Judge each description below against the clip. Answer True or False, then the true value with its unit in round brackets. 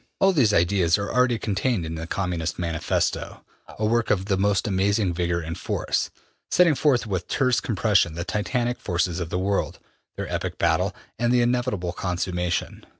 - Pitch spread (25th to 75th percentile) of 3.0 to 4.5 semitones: False (5.1 semitones)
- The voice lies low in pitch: True (100 Hz)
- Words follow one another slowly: False (170 wpm)